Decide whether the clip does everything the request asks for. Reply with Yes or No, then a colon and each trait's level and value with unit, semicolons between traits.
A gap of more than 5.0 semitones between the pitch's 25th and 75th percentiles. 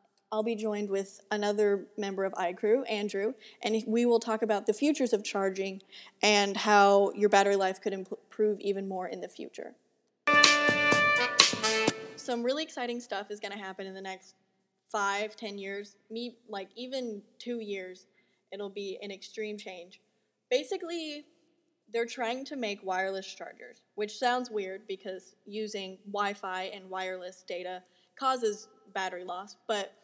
No: average, 3.1 semitones